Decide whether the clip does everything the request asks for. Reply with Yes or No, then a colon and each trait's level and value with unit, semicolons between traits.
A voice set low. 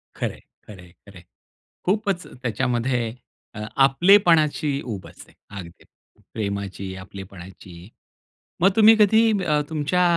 Yes: low, 125 Hz